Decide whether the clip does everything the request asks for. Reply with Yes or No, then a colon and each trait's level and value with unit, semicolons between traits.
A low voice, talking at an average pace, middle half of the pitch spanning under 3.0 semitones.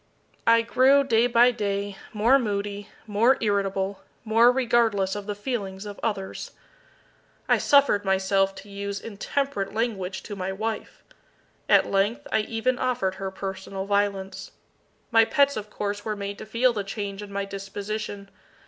No: high, 205 Hz; average, 150 wpm; narrow, 2.6 semitones